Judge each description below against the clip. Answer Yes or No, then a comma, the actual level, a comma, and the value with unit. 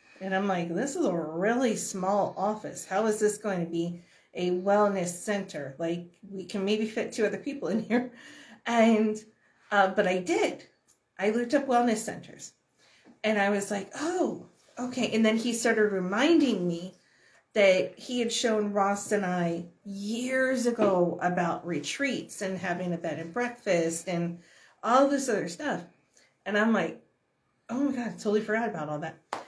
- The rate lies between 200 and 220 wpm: No, average, 170 wpm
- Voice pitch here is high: Yes, high, 205 Hz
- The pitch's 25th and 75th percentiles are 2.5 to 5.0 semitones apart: Yes, average, 4.4 semitones